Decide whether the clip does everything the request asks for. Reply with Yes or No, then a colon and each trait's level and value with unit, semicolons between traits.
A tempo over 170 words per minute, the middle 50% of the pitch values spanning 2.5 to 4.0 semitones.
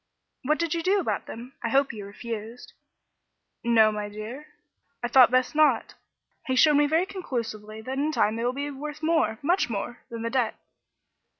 No: average, 185 wpm; average, 5.0 semitones